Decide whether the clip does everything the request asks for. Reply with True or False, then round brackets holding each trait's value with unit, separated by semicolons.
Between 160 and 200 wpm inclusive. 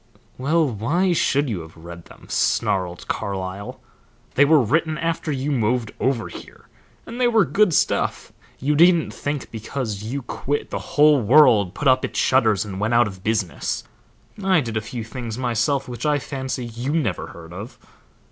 True (175 wpm)